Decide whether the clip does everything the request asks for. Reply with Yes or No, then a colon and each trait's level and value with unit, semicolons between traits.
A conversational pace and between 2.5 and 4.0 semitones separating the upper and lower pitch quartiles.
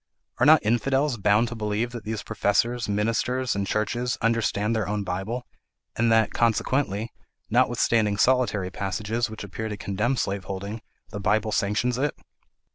Yes: average, 145 wpm; average, 2.8 semitones